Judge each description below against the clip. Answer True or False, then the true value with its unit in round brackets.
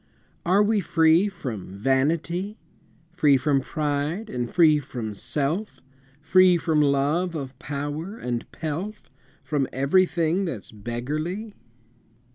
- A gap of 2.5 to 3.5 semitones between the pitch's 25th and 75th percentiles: False (4.7 semitones)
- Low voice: False (155 Hz)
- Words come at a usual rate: False (110 wpm)